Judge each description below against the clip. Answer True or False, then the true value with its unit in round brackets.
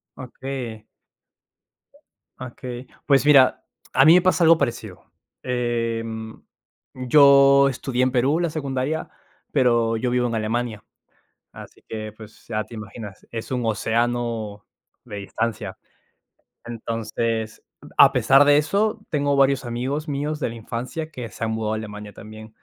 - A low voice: True (120 Hz)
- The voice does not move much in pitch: False (3.6 semitones)